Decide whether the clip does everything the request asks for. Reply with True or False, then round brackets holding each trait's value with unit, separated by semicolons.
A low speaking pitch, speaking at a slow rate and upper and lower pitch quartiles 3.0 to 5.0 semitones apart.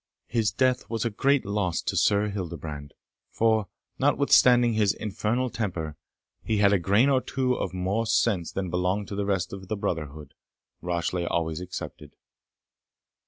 False (100 Hz; 155 wpm; 4.1 semitones)